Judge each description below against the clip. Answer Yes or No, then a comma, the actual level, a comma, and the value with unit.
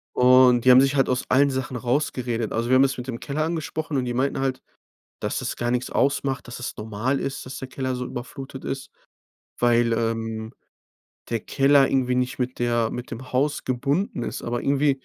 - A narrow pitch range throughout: Yes, narrow, 2.1 semitones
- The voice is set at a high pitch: No, low, 130 Hz